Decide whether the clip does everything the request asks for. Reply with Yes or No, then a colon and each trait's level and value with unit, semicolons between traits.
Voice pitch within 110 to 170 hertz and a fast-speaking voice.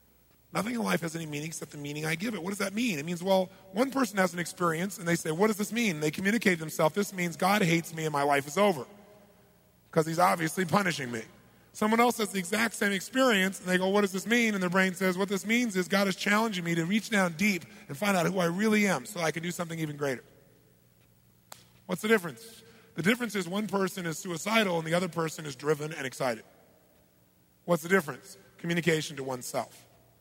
No: medium, 180 Hz; fast, 235 wpm